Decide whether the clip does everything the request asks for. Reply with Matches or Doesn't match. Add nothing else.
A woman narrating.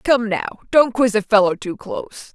Matches